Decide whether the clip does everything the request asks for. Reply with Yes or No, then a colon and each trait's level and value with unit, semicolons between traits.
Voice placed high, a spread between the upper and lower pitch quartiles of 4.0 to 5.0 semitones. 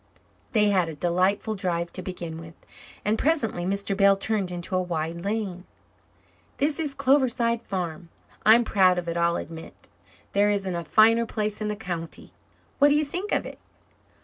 Yes: high, 195 Hz; average, 4.3 semitones